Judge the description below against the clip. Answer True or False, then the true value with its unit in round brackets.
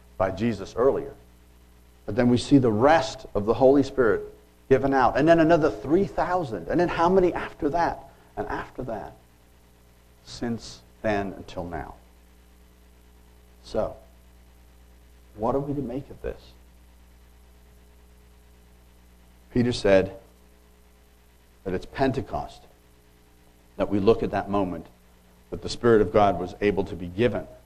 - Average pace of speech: False (130 wpm)